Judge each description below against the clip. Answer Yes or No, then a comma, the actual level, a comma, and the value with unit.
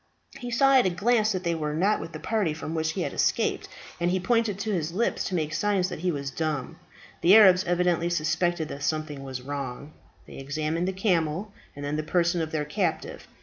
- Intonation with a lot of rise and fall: No, average, 3.8 semitones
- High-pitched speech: No, medium, 170 Hz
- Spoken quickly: Yes, fast, 220 wpm